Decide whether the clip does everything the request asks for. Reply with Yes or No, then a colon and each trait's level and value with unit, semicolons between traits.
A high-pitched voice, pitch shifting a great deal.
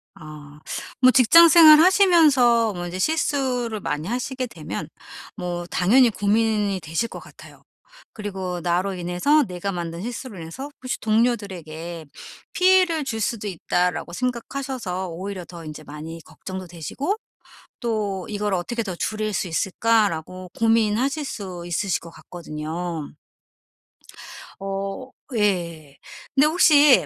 Yes: high, 200 Hz; wide, 6.1 semitones